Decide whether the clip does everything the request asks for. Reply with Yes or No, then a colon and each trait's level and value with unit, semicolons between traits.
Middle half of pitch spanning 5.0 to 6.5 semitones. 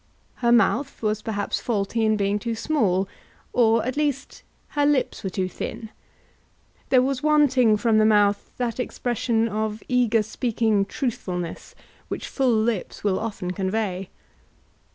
No: average, 3.2 semitones